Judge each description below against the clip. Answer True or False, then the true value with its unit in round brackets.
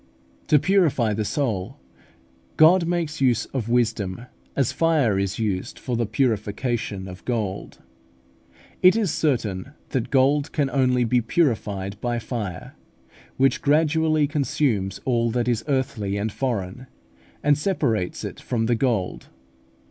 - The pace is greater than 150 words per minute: False (135 wpm)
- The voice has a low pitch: True (120 Hz)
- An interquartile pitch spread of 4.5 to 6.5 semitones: True (5.3 semitones)